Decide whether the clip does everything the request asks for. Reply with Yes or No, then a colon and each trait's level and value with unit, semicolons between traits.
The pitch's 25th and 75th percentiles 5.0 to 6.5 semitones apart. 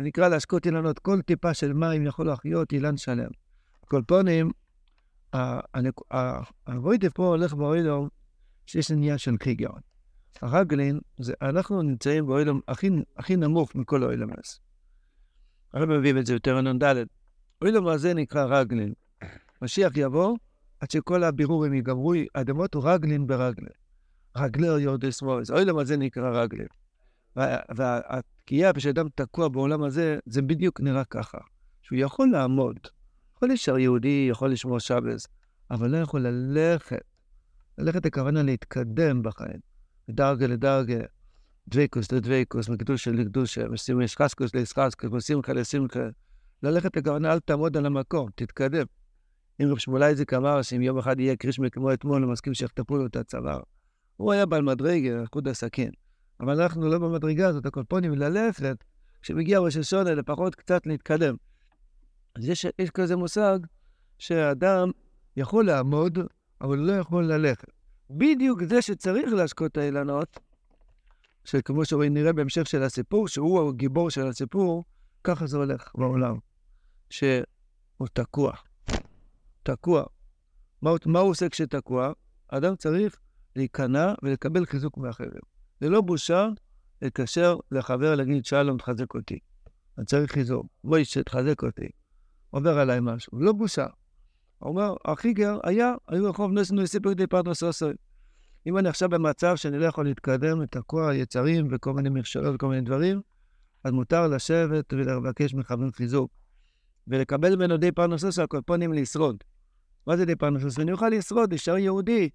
No: average, 4.5 semitones